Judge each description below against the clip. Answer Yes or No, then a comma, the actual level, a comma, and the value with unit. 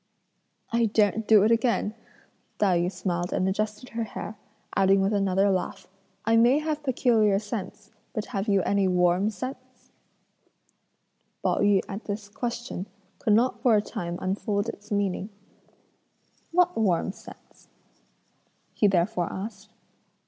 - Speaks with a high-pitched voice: Yes, high, 205 Hz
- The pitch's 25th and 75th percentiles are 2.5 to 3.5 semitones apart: Yes, average, 2.8 semitones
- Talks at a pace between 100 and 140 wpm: Yes, slow, 135 wpm